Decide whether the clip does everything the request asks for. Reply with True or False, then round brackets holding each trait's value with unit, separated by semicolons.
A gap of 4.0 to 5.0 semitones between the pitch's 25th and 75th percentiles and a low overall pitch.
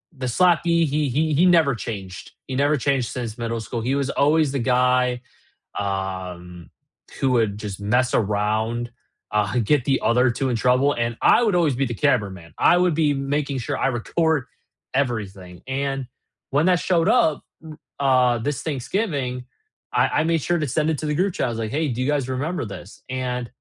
True (4.3 semitones; 130 Hz)